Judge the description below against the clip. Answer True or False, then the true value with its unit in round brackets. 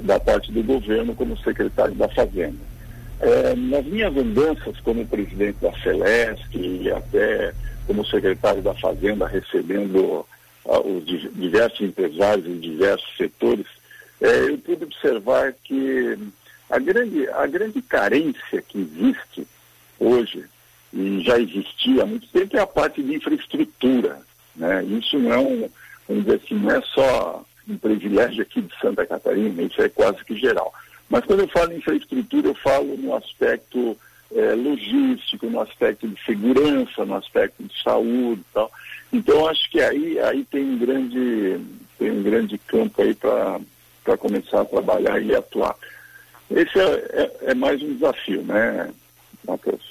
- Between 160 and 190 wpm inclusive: False (150 wpm)